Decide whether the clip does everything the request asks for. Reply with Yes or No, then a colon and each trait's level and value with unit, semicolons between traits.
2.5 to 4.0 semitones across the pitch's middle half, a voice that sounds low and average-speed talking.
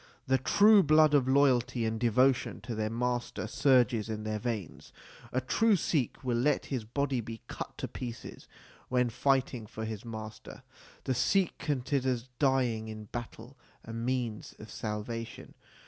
Yes: average, 3.0 semitones; low, 125 Hz; average, 150 wpm